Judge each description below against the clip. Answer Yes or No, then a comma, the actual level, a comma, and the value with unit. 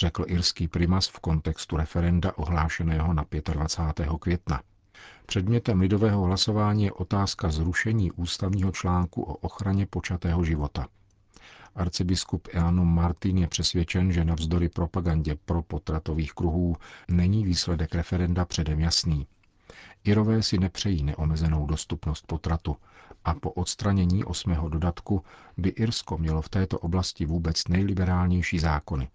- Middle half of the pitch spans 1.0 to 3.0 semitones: Yes, narrow, 2.6 semitones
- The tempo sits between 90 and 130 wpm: Yes, average, 120 wpm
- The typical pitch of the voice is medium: No, very low, 85 Hz